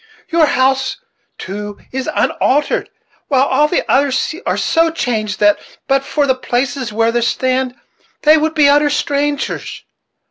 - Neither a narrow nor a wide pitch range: Yes, average, 3.2 semitones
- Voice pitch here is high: Yes, very high, 265 Hz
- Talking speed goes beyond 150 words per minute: No, average, 145 wpm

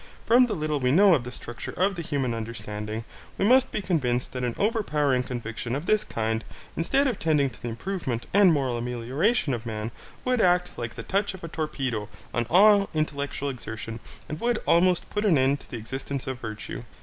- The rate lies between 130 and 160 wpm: No, average, 200 wpm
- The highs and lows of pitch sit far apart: Yes, wide, 7.7 semitones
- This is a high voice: No, medium, 140 Hz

